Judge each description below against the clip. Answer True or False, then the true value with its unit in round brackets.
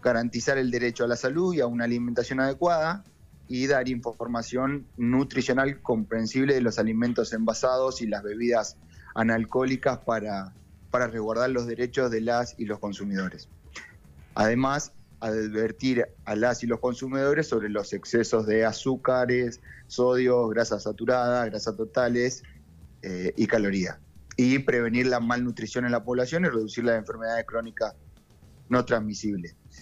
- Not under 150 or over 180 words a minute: False (135 wpm)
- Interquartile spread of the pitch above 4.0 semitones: False (2.5 semitones)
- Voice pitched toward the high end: False (120 Hz)